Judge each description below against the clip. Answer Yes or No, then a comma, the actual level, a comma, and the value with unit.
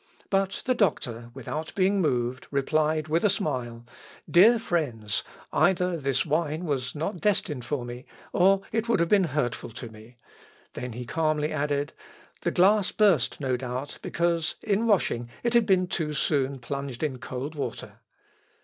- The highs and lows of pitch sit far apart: Yes, wide, 6.4 semitones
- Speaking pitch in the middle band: Yes, medium, 150 Hz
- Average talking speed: Yes, average, 160 wpm